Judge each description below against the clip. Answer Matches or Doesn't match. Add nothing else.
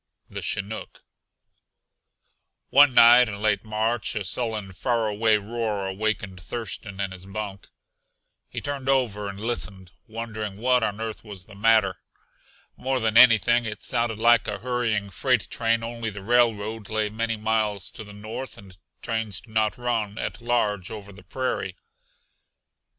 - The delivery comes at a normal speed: Matches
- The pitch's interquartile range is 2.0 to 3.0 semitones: Matches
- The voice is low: Matches